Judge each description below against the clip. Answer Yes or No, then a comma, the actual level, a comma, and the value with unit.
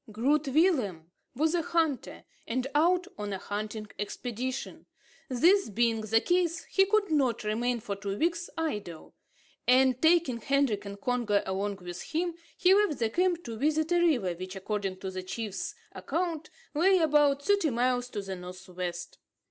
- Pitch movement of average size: No, wide, 7.9 semitones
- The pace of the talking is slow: No, average, 165 wpm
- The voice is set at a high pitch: Yes, very high, 250 Hz